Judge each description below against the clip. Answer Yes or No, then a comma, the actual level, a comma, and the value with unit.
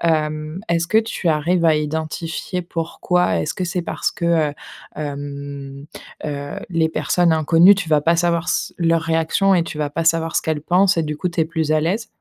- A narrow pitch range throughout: Yes, narrow, 2.1 semitones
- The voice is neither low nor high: Yes, medium, 165 Hz